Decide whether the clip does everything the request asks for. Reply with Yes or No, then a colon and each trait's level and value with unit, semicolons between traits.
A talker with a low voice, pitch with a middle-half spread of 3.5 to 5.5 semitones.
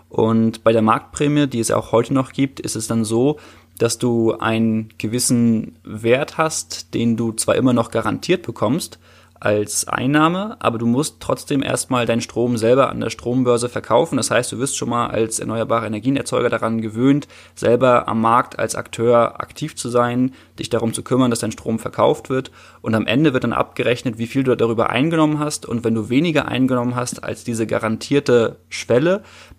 No: low, 120 Hz; average, 2.7 semitones